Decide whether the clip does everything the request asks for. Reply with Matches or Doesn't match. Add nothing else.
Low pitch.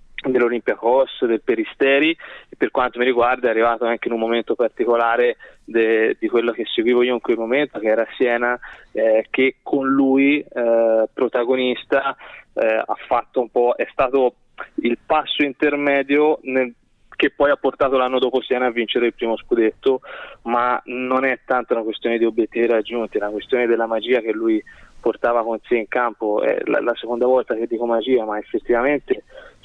Matches